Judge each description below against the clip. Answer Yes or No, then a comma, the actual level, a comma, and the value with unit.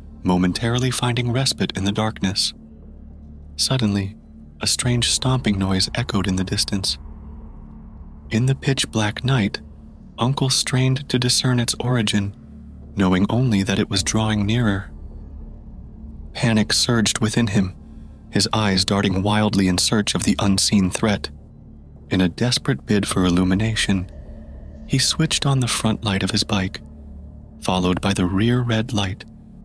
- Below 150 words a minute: Yes, average, 140 wpm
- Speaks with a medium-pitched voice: No, low, 100 Hz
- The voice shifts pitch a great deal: Yes, wide, 7.4 semitones